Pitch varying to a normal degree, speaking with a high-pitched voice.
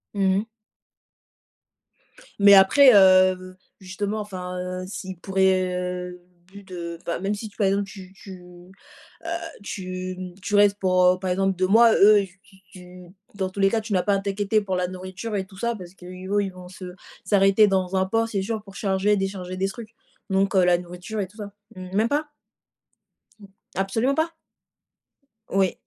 No: narrow, 1.8 semitones; high, 195 Hz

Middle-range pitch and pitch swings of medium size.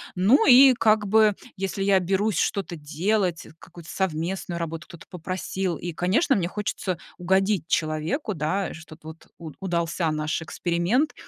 Yes: medium, 180 Hz; average, 3.3 semitones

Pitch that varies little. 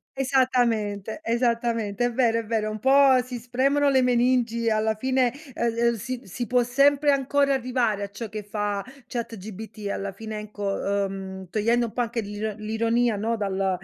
No: average, 3.0 semitones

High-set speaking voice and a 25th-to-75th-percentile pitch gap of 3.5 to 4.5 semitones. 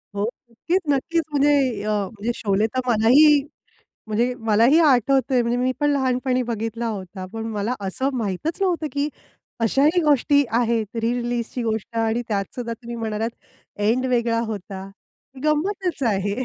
Yes: high, 235 Hz; average, 3.9 semitones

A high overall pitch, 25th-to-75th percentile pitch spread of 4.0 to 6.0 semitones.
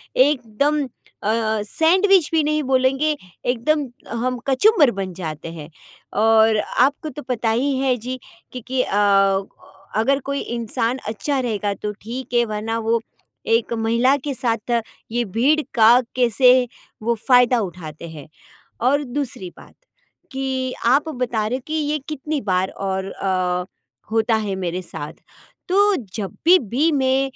Yes: high, 245 Hz; average, 4.3 semitones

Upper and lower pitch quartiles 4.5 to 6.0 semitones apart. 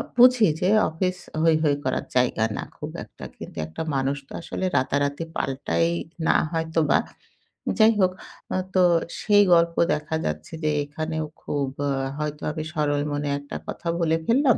No: average, 3.4 semitones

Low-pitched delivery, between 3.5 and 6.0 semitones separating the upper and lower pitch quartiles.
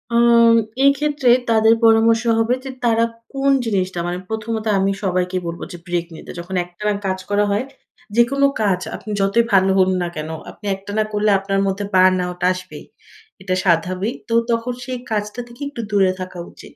No: high, 205 Hz; average, 3.8 semitones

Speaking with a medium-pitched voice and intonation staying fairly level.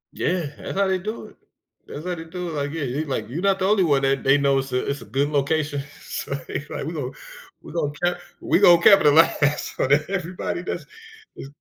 No: medium, 150 Hz; average, 4.2 semitones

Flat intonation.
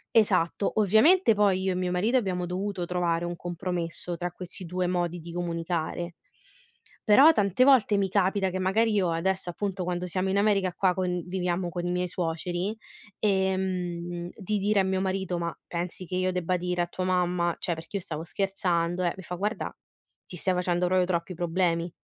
Yes: narrow, 1.7 semitones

